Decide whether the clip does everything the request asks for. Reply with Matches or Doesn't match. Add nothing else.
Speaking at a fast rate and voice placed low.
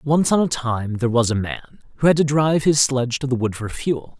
Matches